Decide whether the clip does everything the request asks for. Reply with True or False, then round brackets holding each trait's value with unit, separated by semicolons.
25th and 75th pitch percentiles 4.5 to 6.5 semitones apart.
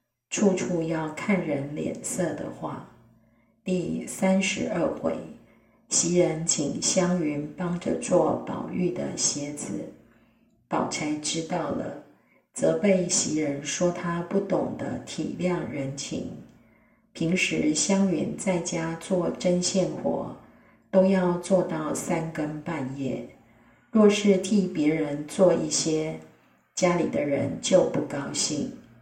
False (3.8 semitones)